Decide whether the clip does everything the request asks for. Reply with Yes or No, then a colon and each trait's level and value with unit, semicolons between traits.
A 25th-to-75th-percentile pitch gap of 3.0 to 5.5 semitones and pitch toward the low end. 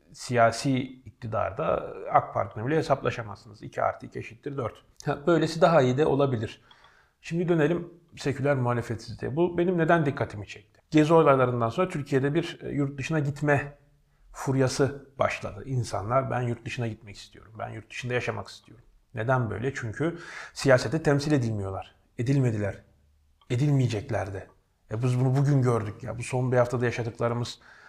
Yes: average, 4.4 semitones; low, 125 Hz